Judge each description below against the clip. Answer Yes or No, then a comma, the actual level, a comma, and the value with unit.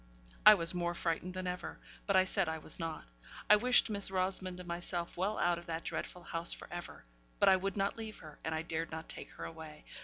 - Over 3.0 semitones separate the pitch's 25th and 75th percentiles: No, narrow, 2.5 semitones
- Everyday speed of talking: No, fast, 235 wpm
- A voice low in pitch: No, medium, 175 Hz